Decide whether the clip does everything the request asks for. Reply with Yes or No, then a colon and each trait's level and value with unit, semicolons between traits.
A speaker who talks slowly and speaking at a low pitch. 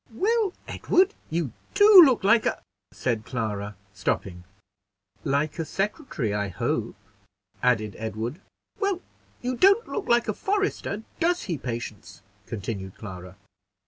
No: slow, 130 wpm; medium, 150 Hz